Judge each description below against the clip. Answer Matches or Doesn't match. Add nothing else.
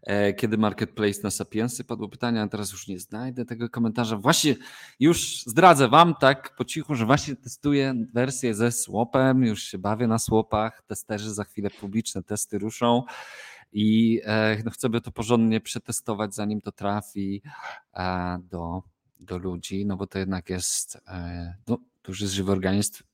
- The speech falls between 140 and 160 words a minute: Matches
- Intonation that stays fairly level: Doesn't match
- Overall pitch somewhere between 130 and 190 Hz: Doesn't match